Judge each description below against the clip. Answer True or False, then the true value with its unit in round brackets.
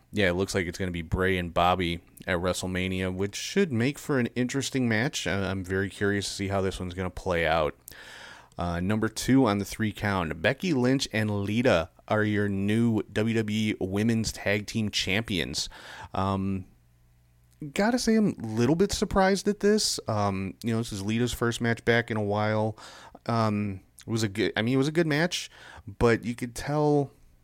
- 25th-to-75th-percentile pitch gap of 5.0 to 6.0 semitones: False (4.3 semitones)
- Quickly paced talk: False (195 wpm)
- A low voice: True (105 Hz)